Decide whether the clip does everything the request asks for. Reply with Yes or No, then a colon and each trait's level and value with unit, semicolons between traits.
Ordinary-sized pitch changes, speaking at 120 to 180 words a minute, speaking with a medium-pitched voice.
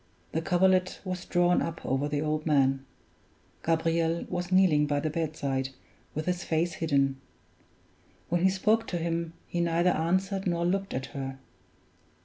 Yes: average, 3.2 semitones; average, 150 wpm; medium, 165 Hz